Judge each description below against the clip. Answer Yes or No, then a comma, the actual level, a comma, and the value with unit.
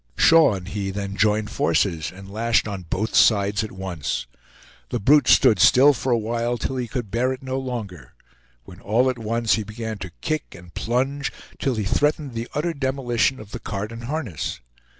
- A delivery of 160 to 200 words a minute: Yes, average, 190 wpm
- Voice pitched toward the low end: Yes, low, 115 Hz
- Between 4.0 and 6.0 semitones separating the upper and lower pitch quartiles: Yes, average, 4.7 semitones